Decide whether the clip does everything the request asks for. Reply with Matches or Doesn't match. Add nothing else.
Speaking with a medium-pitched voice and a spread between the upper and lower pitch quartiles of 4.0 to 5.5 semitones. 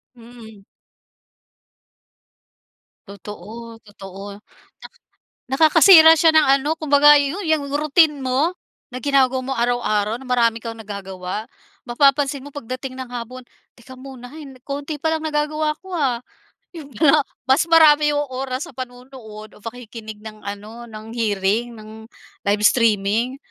Doesn't match